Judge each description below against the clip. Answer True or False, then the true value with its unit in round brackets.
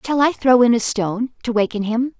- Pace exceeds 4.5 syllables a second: True (5.6 syllables/s)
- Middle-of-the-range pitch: False (235 Hz)